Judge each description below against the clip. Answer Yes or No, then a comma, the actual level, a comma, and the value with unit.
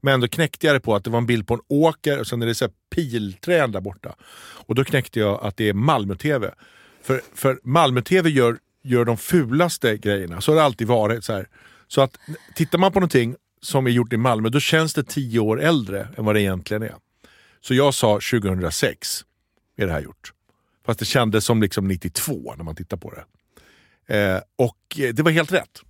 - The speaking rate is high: Yes, fast, 215 wpm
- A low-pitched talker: Yes, low, 120 Hz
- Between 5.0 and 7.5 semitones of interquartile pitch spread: Yes, wide, 5.4 semitones